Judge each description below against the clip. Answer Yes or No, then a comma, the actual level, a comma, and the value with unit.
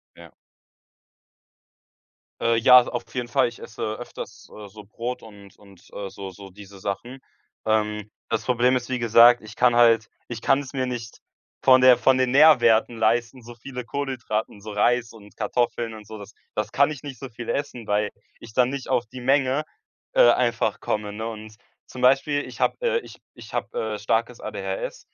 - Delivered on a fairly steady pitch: No, average, 3.0 semitones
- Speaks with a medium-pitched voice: No, low, 120 Hz